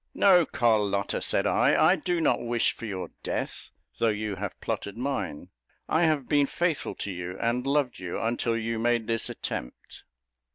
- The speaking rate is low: No, average, 170 wpm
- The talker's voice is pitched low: Yes, low, 115 Hz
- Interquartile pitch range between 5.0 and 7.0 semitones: Yes, wide, 5.5 semitones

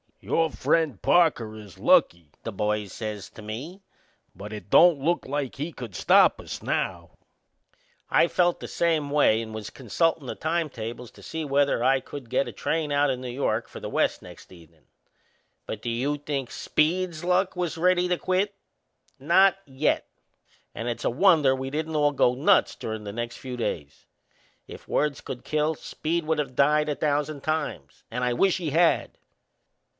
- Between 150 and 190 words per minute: Yes, average, 180 wpm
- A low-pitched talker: No, medium, 145 Hz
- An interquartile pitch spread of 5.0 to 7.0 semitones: Yes, wide, 5.5 semitones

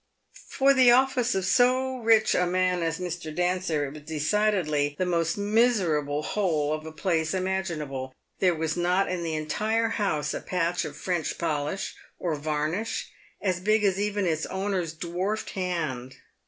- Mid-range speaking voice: Yes, medium, 180 Hz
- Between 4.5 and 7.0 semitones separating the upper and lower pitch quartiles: Yes, average, 4.8 semitones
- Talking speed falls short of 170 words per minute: Yes, average, 160 wpm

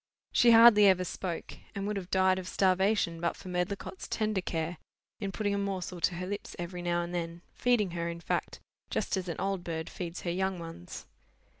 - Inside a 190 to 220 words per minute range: Yes, average, 200 wpm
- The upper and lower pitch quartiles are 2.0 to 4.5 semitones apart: Yes, narrow, 2.4 semitones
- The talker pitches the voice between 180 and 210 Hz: Yes, medium, 185 Hz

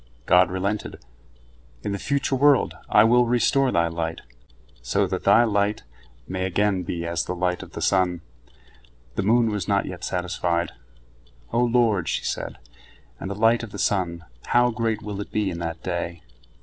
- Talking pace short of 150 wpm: No, average, 175 wpm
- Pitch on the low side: Yes, low, 100 Hz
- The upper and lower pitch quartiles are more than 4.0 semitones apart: Yes, average, 4.6 semitones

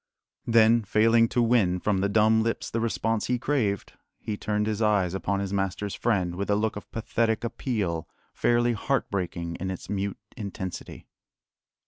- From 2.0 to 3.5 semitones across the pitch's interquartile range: Yes, average, 2.8 semitones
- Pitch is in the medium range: No, low, 105 Hz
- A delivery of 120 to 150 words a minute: No, average, 160 wpm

